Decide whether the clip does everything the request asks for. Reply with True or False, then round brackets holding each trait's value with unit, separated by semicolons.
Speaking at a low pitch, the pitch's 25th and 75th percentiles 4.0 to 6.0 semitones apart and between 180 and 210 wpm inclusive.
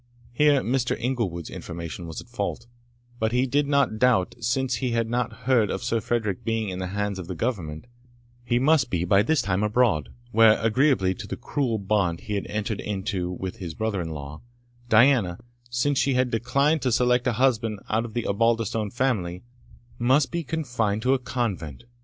True (115 Hz; 4.5 semitones; 190 wpm)